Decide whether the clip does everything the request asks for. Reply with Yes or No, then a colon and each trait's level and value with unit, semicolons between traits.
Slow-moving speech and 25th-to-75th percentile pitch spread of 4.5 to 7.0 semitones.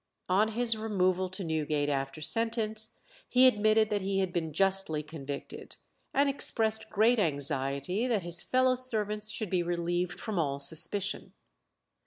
No: average, 145 wpm; average, 5.3 semitones